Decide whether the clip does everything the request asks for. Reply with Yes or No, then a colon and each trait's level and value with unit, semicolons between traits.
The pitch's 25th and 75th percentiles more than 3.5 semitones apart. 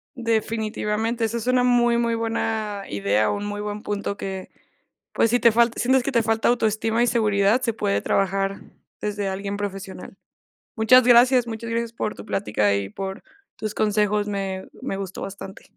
No: average, 2.8 semitones